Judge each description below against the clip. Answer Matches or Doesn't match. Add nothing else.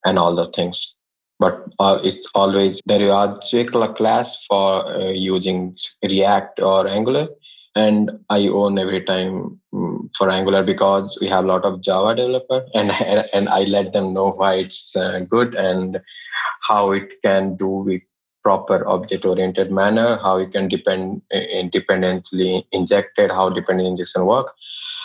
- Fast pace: Doesn't match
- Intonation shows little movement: Matches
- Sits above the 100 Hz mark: Doesn't match